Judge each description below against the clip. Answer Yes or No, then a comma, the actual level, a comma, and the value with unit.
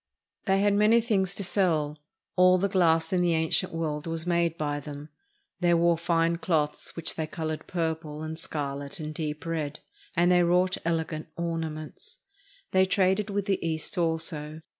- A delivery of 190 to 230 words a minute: No, average, 165 wpm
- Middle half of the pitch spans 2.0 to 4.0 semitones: Yes, average, 2.7 semitones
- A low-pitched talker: No, medium, 165 Hz